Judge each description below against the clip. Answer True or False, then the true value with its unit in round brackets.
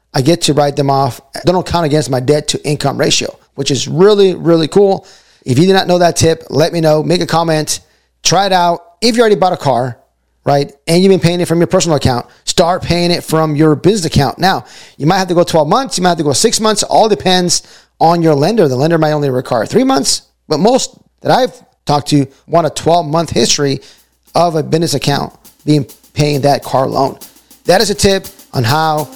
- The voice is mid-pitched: True (160 Hz)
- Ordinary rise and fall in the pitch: True (3.8 semitones)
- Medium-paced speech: False (230 wpm)